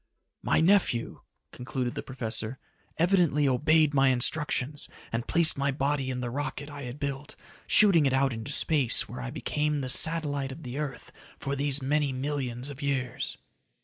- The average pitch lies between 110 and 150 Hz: Yes, medium, 140 Hz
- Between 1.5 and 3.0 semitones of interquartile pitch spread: Yes, narrow, 2.5 semitones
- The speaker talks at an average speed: Yes, average, 165 wpm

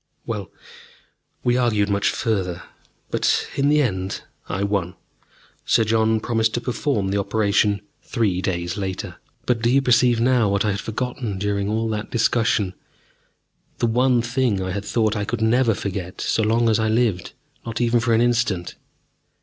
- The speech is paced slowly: No, average, 165 wpm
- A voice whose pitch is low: Yes, low, 110 Hz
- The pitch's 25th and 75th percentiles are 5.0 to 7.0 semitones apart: No, average, 2.9 semitones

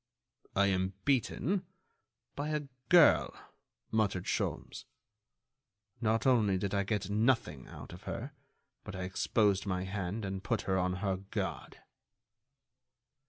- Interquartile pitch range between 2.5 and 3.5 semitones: Yes, average, 3.2 semitones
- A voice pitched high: No, low, 100 Hz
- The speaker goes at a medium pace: No, slow, 125 wpm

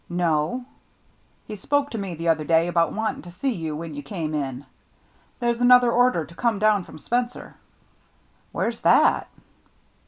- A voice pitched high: No, medium, 175 Hz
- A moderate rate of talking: Yes, average, 175 wpm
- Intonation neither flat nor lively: No, wide, 6.9 semitones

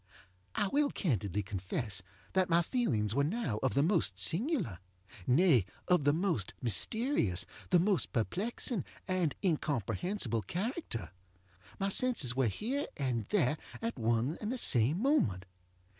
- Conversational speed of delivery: No, slow, 130 wpm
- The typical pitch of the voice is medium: Yes, medium, 145 Hz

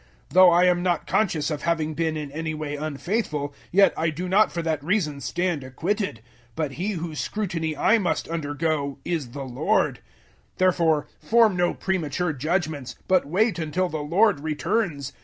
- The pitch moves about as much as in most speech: Yes, average, 3.6 semitones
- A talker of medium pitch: Yes, medium, 165 Hz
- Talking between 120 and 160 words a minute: No, average, 175 wpm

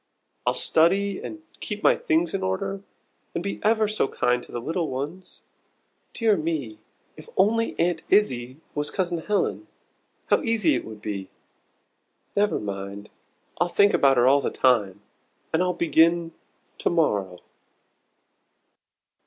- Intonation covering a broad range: Yes, wide, 8.2 semitones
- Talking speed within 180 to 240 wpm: No, average, 140 wpm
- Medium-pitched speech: Yes, medium, 165 Hz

